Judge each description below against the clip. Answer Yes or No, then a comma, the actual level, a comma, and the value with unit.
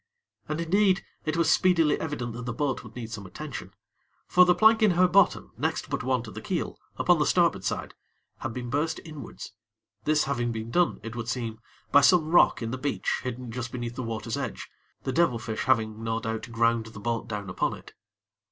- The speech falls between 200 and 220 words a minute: Yes, fast, 205 wpm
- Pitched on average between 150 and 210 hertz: No, low, 125 Hz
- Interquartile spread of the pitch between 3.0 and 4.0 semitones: No, wide, 5.5 semitones